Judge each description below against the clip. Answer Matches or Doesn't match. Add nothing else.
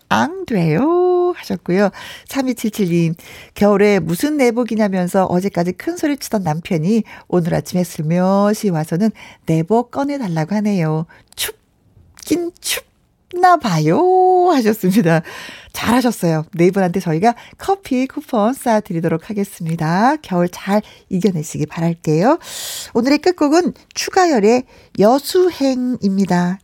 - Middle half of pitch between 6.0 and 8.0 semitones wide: Matches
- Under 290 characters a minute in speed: Matches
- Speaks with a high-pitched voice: Matches